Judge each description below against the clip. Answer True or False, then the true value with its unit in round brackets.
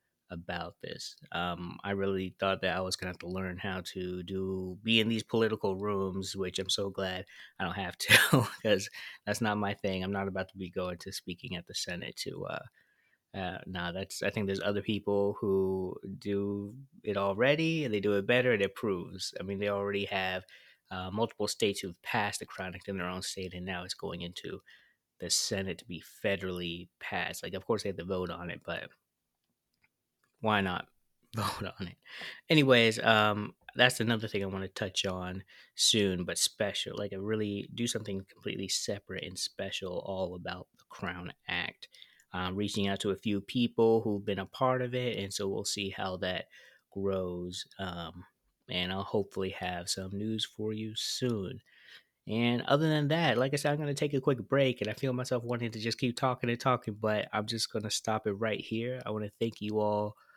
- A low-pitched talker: True (100 Hz)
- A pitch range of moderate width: True (3.0 semitones)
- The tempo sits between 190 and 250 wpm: True (205 wpm)